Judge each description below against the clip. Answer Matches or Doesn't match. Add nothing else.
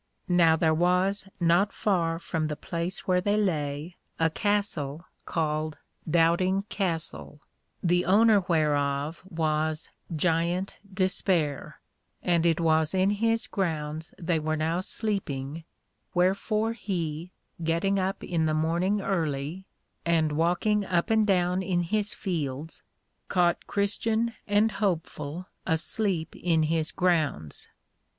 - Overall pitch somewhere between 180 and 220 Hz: Doesn't match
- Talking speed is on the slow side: Matches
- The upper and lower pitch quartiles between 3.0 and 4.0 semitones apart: Matches